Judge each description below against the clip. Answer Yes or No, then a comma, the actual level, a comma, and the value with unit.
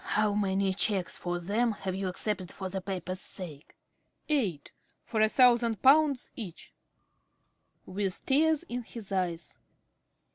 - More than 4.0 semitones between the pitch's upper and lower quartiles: Yes, average, 4.4 semitones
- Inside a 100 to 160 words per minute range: Yes, average, 145 wpm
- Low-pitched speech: No, high, 200 Hz